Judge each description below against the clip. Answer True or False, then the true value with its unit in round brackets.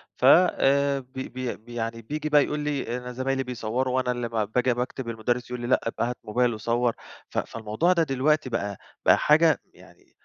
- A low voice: True (125 Hz)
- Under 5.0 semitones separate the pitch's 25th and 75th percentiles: True (2.8 semitones)